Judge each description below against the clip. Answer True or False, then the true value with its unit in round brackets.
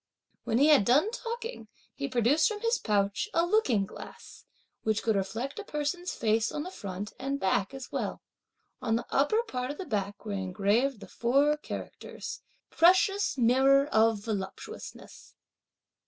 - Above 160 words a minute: False (155 wpm)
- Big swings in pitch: True (6.4 semitones)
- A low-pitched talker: False (260 Hz)